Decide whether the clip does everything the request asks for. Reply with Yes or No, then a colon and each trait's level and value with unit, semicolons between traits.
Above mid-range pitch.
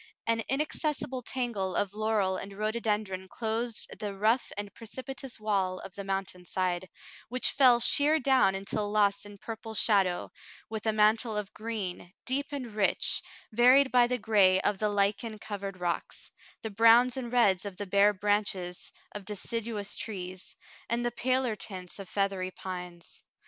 Yes: high, 210 Hz